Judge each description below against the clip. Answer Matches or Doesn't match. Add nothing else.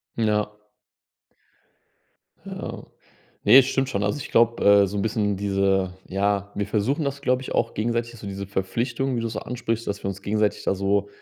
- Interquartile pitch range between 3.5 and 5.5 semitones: Doesn't match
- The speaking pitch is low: Matches